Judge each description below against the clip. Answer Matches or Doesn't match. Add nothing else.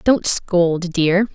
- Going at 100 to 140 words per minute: Matches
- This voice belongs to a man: Doesn't match